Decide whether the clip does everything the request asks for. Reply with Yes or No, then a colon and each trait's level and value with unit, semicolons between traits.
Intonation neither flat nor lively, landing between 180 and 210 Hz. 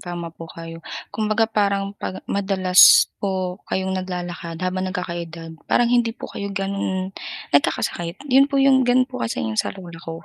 Yes: average, 3.5 semitones; high, 190 Hz